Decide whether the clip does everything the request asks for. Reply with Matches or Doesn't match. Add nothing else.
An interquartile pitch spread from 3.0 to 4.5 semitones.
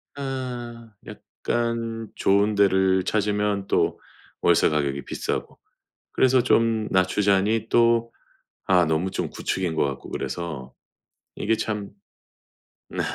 Matches